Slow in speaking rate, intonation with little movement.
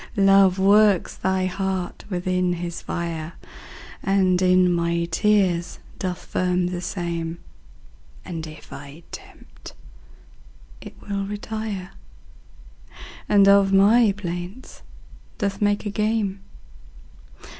Yes: slow, 100 wpm; narrow, 2.2 semitones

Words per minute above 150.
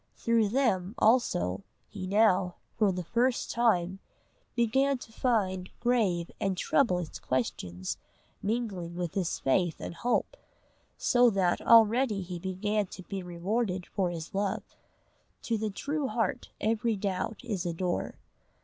No: slow, 135 wpm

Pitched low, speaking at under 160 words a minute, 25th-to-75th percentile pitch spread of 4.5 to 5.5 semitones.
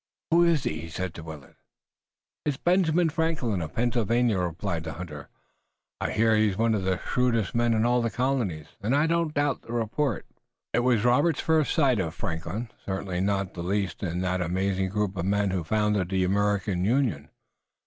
No: low, 105 Hz; average, 185 wpm; average, 5.2 semitones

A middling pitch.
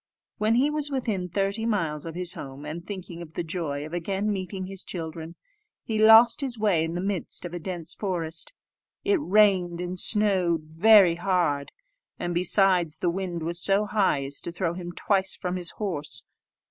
Yes: medium, 180 Hz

